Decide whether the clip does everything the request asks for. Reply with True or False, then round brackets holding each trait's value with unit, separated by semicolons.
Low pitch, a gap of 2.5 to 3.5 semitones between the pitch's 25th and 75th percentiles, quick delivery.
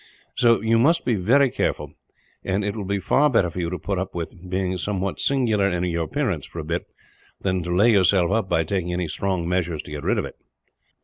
True (95 Hz; 3.2 semitones; 230 wpm)